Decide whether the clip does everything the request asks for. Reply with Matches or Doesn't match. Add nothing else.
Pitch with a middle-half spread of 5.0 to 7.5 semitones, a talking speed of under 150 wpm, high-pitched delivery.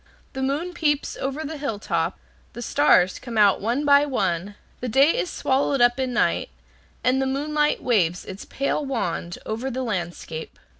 Doesn't match